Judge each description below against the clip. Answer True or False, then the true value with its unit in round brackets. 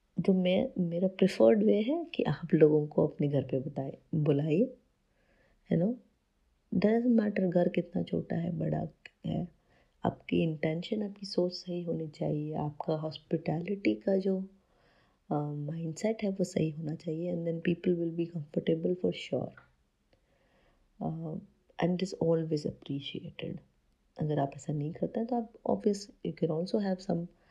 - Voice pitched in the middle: True (170 Hz)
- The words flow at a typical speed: True (150 wpm)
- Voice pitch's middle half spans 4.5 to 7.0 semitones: False (4.1 semitones)